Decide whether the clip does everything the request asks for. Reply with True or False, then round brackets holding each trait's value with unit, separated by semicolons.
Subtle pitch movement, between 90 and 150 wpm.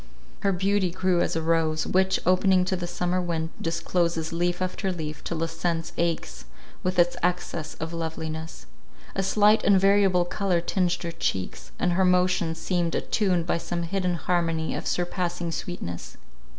False (1.9 semitones; 165 wpm)